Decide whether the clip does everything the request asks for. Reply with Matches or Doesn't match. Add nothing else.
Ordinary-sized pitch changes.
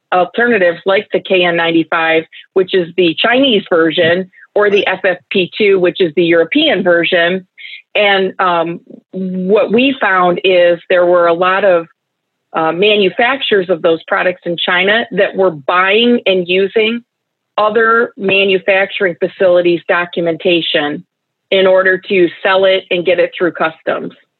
Doesn't match